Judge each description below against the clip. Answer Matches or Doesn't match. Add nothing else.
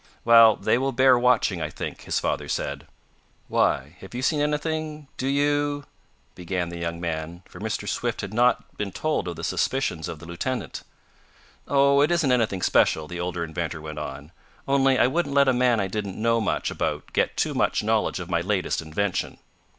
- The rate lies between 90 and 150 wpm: Doesn't match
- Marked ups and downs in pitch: Matches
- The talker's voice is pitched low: Matches